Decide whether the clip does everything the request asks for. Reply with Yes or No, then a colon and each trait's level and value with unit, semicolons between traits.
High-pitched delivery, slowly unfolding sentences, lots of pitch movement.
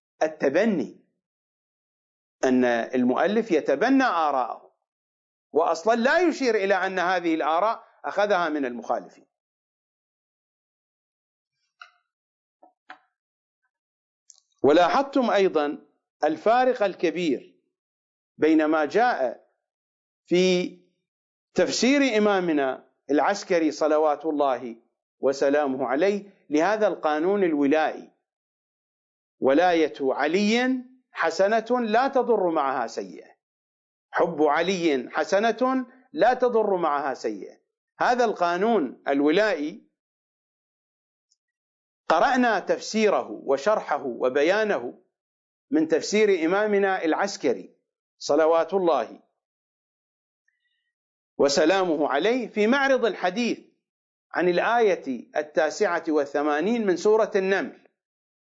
Yes: high, 195 Hz; slow, 75 wpm; wide, 7.6 semitones